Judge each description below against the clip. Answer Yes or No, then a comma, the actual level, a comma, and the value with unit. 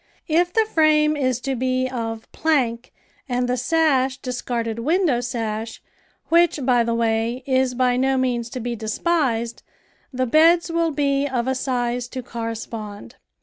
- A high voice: Yes, very high, 255 Hz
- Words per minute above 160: No, average, 150 wpm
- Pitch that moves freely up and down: No, average, 3.4 semitones